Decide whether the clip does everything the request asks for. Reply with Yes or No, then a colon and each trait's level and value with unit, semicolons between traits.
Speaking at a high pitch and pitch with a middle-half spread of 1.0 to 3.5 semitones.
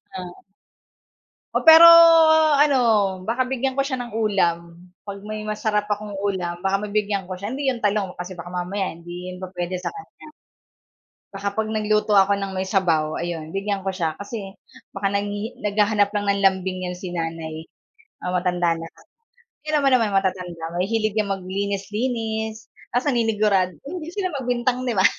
Yes: high, 200 Hz; average, 3.2 semitones